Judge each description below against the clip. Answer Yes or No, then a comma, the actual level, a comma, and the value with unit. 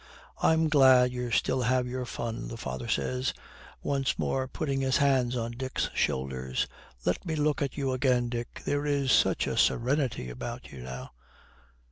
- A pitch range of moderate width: Yes, average, 3.1 semitones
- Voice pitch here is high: No, low, 125 Hz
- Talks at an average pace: Yes, average, 165 wpm